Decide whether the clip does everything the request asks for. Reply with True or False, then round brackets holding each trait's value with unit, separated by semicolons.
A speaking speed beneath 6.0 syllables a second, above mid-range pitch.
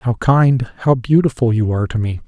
False (5.0 syllables/s; 120 Hz)